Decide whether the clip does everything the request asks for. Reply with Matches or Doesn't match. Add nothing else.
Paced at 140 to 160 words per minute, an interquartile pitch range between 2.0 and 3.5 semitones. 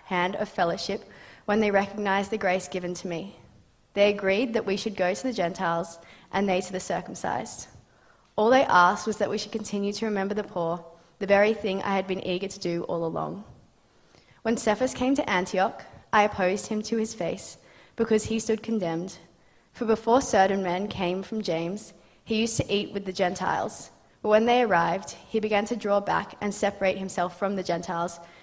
Doesn't match